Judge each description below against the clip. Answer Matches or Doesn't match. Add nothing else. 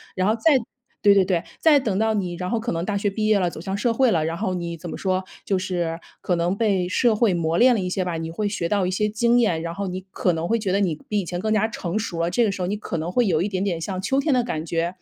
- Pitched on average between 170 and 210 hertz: Matches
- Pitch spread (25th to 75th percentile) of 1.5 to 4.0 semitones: Matches